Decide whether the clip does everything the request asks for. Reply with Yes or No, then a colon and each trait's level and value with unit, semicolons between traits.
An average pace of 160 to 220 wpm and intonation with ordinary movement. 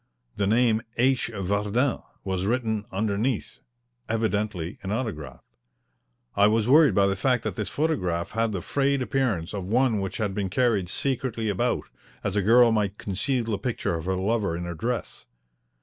Yes: average, 165 wpm; average, 3.9 semitones